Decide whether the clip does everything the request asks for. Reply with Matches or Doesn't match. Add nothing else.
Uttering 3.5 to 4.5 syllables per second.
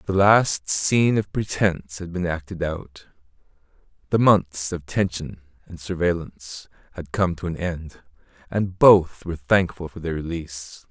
Matches